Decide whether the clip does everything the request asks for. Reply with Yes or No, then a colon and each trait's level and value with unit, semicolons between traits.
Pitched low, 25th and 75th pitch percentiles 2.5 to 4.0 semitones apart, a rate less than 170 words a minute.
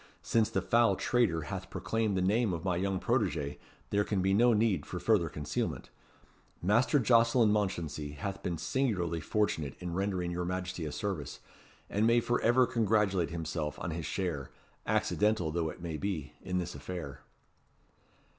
No: very low, 95 Hz; average, 4.7 semitones; average, 160 wpm